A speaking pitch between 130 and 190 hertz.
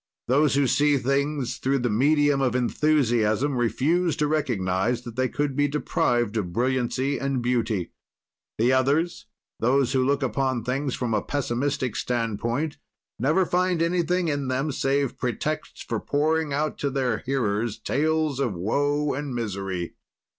Yes: low, 135 Hz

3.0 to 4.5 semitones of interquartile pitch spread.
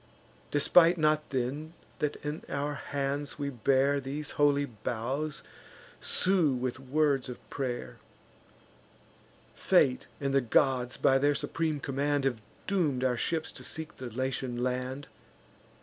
No: narrow, 2.4 semitones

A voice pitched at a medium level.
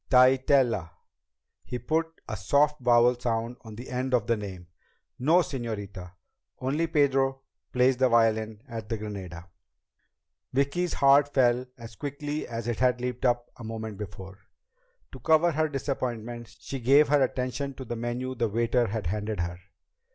No: low, 120 Hz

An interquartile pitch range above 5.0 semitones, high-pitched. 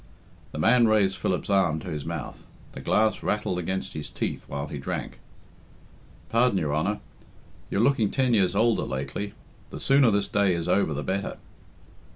No: wide, 5.6 semitones; low, 100 Hz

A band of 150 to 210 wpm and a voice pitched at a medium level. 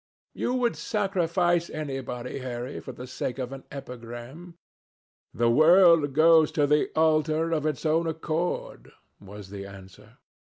No: slow, 135 wpm; medium, 155 Hz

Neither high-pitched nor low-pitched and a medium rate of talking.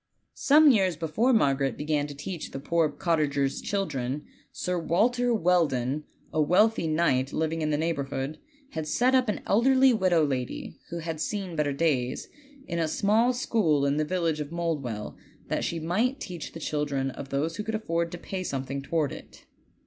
Yes: medium, 165 Hz; average, 175 wpm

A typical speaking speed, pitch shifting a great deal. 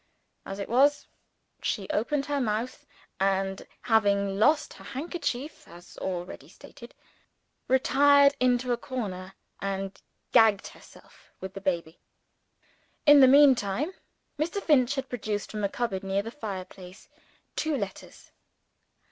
No: slow, 125 wpm; wide, 5.9 semitones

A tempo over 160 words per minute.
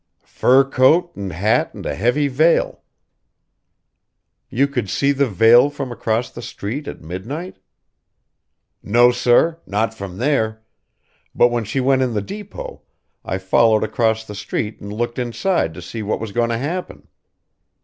No: average, 155 wpm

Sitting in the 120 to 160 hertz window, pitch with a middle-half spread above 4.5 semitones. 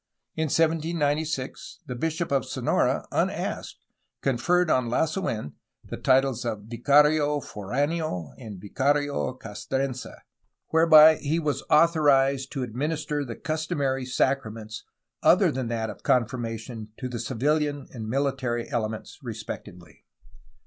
No: low, 135 Hz; average, 4.2 semitones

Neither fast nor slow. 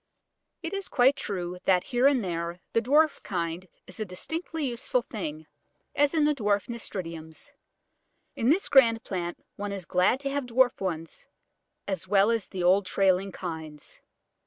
Yes: average, 160 wpm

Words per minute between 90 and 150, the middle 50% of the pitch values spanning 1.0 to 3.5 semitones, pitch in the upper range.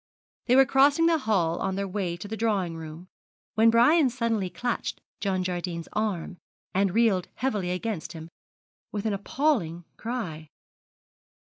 No: average, 145 wpm; average, 4.7 semitones; high, 200 Hz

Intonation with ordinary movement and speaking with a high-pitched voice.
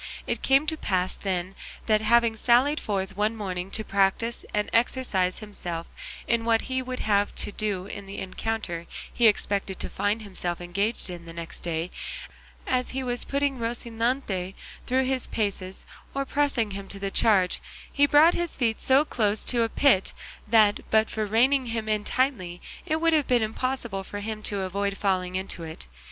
Yes: average, 4.3 semitones; high, 215 Hz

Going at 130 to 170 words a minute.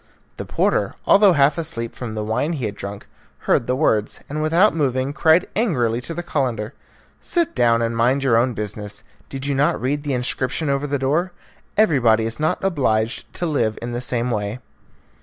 No: average, 190 wpm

